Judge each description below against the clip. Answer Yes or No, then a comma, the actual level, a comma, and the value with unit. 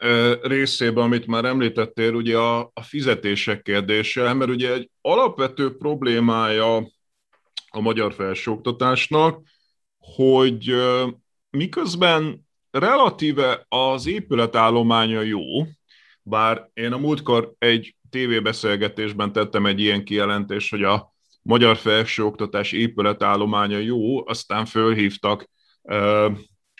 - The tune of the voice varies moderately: Yes, average, 3.0 semitones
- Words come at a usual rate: No, slow, 90 wpm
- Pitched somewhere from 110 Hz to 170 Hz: Yes, low, 115 Hz